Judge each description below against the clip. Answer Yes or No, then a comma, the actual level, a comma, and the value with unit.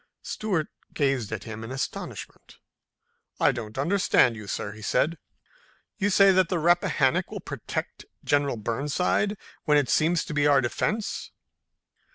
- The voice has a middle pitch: Yes, medium, 145 Hz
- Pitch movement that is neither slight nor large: No, wide, 6.7 semitones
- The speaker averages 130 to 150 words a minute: Yes, average, 145 wpm